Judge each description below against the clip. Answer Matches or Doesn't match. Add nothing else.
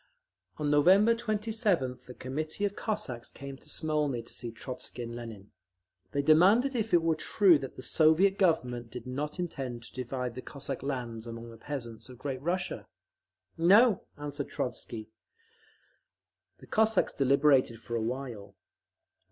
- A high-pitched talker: Doesn't match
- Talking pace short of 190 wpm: Matches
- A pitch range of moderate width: Doesn't match